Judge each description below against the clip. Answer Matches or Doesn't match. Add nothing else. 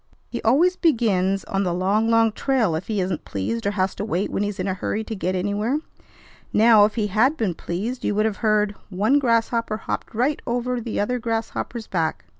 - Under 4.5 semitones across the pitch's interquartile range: Matches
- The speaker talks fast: Matches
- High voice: Matches